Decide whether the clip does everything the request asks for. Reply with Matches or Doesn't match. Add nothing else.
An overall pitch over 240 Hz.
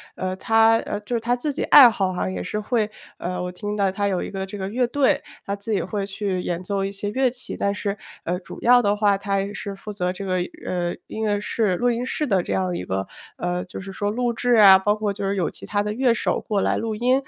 Doesn't match